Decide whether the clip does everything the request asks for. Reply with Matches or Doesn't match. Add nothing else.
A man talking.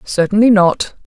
Doesn't match